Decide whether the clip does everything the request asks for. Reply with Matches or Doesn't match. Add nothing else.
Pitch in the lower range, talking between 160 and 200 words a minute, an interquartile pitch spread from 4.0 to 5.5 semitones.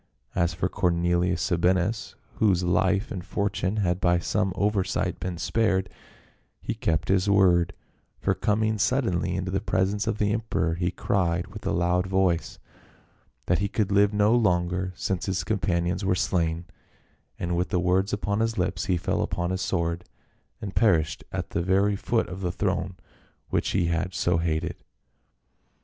Doesn't match